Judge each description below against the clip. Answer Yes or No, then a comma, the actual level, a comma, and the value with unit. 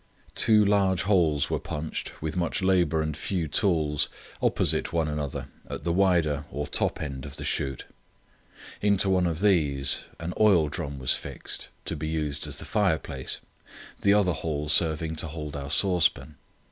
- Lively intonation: No, average, 3.8 semitones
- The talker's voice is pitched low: Yes, very low, 80 Hz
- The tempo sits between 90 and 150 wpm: No, average, 165 wpm